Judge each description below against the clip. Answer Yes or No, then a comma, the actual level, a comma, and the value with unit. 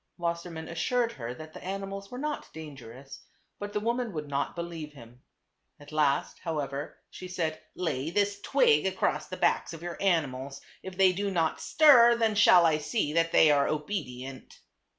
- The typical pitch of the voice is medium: Yes, medium, 165 Hz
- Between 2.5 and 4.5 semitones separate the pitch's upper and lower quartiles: No, average, 5.1 semitones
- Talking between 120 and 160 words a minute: No, average, 170 wpm